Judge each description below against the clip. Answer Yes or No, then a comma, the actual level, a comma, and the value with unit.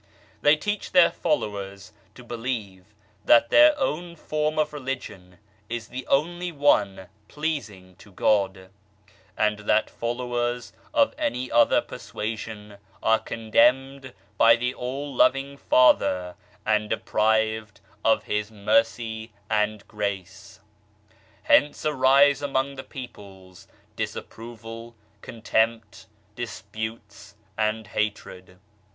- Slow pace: Yes, slow, 105 wpm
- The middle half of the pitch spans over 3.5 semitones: Yes, average, 4.2 semitones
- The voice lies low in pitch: Yes, low, 115 Hz